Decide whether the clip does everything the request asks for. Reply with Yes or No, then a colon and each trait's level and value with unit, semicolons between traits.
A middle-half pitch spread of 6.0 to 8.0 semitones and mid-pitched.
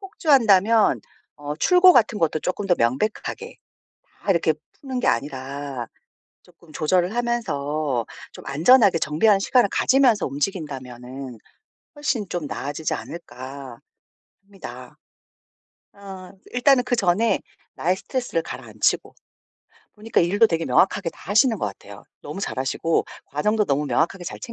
Yes: wide, 7.4 semitones; medium, 180 Hz